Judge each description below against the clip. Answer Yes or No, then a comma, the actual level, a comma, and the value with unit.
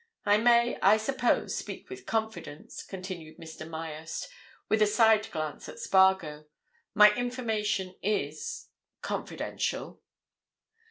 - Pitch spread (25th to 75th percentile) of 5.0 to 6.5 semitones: Yes, wide, 5.4 semitones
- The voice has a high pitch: Yes, high, 205 Hz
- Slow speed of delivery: Yes, slow, 105 wpm